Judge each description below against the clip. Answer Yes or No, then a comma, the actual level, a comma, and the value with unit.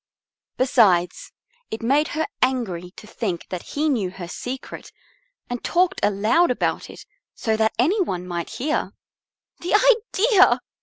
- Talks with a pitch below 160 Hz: No, high, 245 Hz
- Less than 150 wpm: Yes, average, 140 wpm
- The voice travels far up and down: Yes, wide, 8.5 semitones